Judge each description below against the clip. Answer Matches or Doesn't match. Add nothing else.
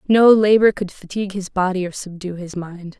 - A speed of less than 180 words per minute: Doesn't match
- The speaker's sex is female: Matches